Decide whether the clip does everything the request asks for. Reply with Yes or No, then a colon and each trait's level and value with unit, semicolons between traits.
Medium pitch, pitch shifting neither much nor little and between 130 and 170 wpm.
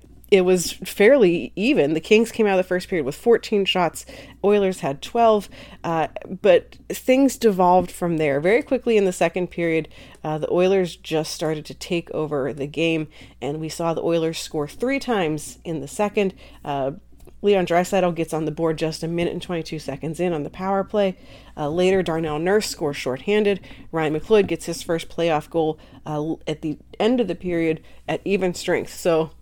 No: medium, 170 Hz; average, 3.9 semitones; average, 190 wpm